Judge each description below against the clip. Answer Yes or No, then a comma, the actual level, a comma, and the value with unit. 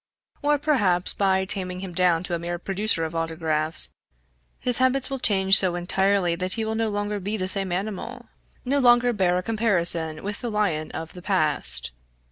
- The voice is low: No, high, 190 Hz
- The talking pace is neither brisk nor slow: Yes, average, 185 wpm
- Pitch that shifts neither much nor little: Yes, average, 3.9 semitones